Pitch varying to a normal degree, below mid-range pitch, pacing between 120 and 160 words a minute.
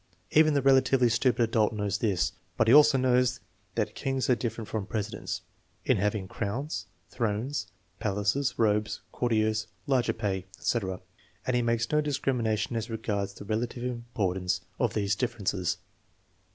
Yes: average, 3.5 semitones; low, 115 Hz; average, 145 wpm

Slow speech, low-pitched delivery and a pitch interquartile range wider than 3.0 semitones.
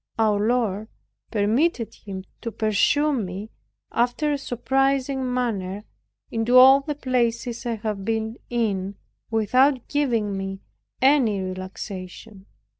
No: slow, 115 wpm; high, 225 Hz; average, 4.0 semitones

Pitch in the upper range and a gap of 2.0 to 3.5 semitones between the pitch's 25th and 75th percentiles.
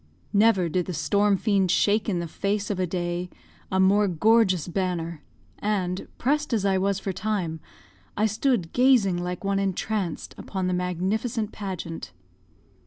Yes: high, 195 Hz; average, 2.8 semitones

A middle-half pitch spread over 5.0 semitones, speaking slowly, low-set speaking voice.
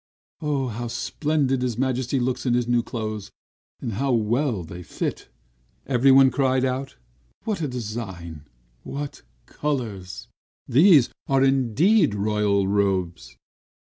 No: average, 4.3 semitones; slow, 115 wpm; low, 125 Hz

